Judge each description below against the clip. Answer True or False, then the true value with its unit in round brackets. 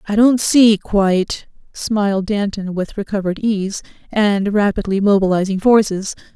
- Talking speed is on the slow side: True (125 wpm)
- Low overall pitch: False (200 Hz)